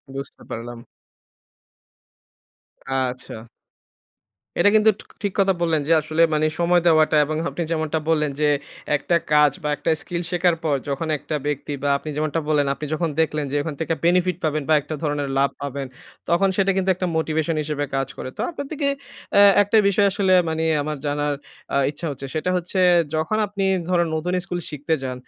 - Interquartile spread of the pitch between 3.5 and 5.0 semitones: No, average, 3.1 semitones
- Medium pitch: Yes, medium, 155 Hz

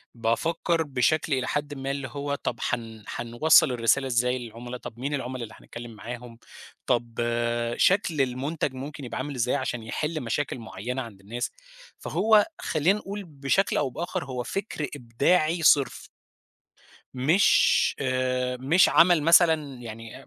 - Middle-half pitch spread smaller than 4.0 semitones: No, average, 4.3 semitones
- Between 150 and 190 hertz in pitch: No, low, 130 Hz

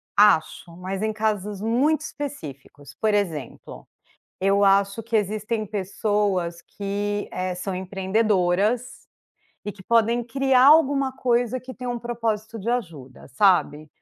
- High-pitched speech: Yes, high, 210 Hz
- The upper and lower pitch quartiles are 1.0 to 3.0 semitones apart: No, average, 4.0 semitones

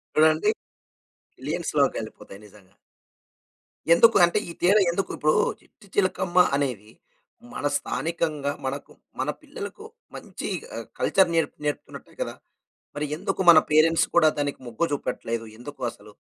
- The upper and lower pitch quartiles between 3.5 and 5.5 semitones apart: Yes, average, 3.8 semitones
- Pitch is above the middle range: No, medium, 155 Hz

